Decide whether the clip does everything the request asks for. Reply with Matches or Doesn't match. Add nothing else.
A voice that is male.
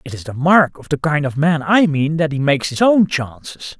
Matches